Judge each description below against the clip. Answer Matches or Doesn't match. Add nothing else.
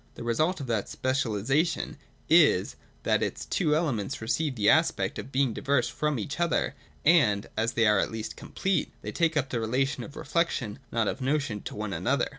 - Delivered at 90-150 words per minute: Doesn't match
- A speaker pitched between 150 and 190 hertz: Doesn't match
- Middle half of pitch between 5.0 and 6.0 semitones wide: Matches